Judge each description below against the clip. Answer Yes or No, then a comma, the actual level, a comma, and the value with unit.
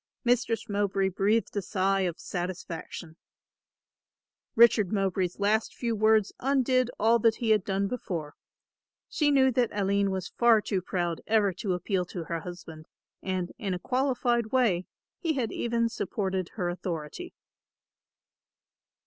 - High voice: Yes, high, 200 Hz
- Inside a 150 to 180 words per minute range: No, average, 140 wpm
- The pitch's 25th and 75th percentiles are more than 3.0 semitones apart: Yes, average, 4.1 semitones